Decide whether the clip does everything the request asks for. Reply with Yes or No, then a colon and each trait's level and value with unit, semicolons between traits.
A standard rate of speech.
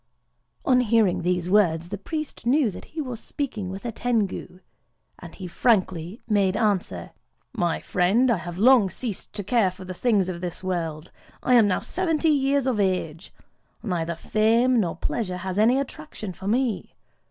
Yes: average, 165 wpm